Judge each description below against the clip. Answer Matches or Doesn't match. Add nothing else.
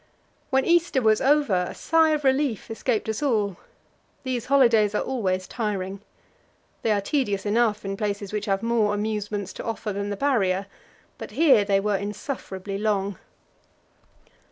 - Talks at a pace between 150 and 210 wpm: Matches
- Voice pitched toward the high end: Matches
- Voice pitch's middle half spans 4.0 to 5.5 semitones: Matches